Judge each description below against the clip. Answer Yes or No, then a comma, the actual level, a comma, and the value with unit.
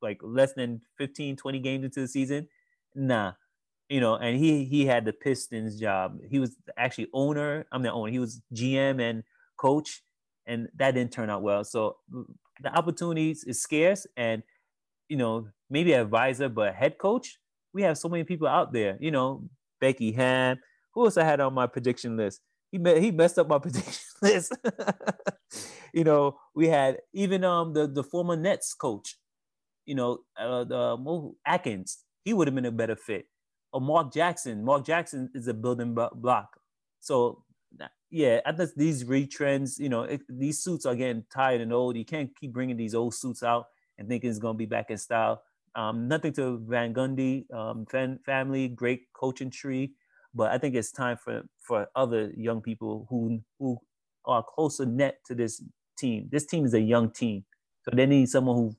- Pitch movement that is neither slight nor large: Yes, average, 3.8 semitones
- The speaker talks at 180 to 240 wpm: Yes, average, 185 wpm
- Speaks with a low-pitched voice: Yes, low, 130 Hz